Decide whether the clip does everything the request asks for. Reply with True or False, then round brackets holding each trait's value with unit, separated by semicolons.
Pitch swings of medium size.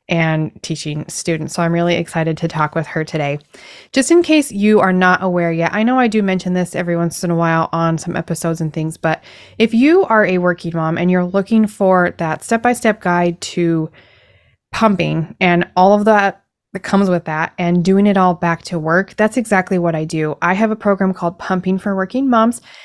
True (3.4 semitones)